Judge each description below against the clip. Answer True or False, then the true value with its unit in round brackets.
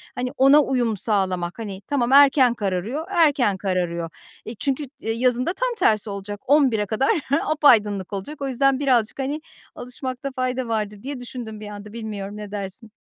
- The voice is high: True (235 Hz)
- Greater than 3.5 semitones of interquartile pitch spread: True (4.7 semitones)